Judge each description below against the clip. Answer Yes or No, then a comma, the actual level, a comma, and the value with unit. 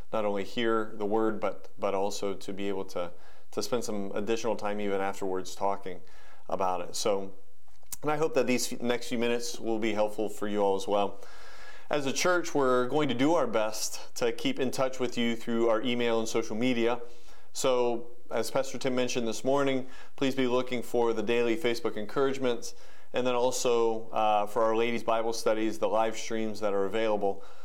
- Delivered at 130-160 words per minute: No, average, 195 wpm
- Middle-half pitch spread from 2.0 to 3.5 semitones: Yes, average, 2.8 semitones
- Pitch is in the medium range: No, low, 115 Hz